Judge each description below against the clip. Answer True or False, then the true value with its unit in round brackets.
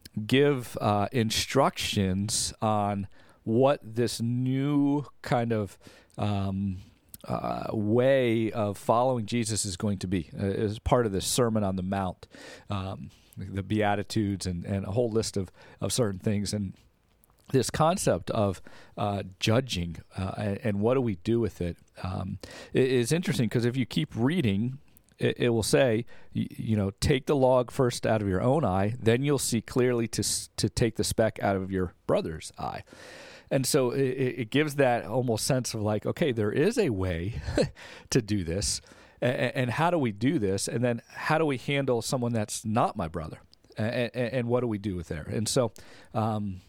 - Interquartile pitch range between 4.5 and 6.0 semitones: False (3.9 semitones)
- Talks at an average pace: True (175 wpm)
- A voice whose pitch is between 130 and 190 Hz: False (110 Hz)